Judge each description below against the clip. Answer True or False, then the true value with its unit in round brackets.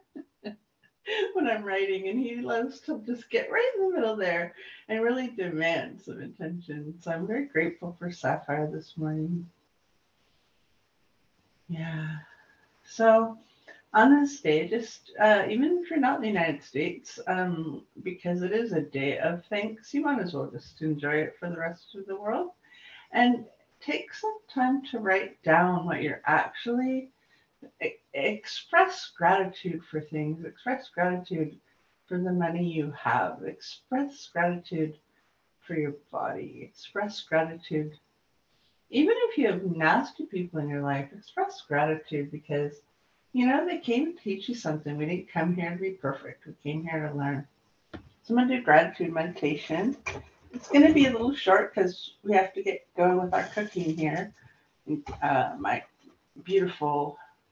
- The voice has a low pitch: False (185 Hz)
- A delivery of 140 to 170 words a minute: True (155 wpm)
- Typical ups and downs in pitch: False (7.7 semitones)